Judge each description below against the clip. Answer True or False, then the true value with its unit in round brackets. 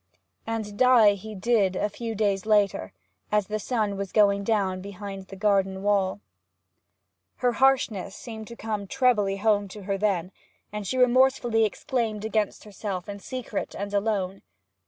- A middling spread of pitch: False (2.2 semitones)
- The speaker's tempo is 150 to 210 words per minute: True (155 wpm)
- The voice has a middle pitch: False (210 Hz)